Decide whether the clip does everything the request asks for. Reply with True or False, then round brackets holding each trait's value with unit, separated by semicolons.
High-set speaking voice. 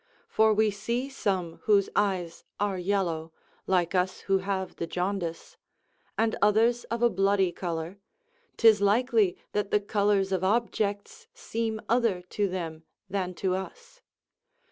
True (200 Hz)